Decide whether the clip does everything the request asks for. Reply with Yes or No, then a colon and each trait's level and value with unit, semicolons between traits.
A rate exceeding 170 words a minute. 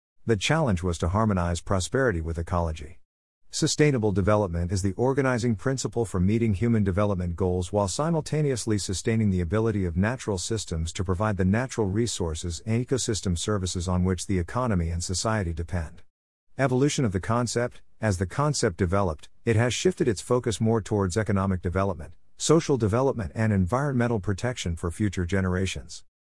No: average, 155 wpm